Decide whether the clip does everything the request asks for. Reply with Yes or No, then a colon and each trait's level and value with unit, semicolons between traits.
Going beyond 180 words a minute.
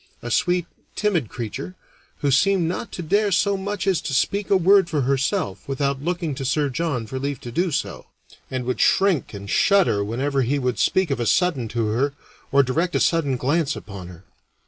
Yes: average, 200 wpm